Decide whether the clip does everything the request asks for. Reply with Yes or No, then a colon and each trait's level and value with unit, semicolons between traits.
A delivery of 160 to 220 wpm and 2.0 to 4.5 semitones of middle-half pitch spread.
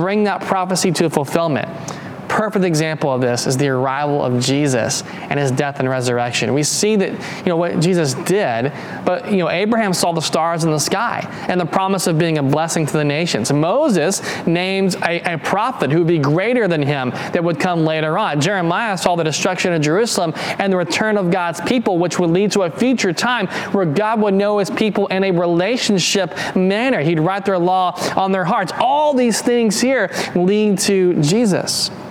Yes: average, 200 wpm; average, 3.9 semitones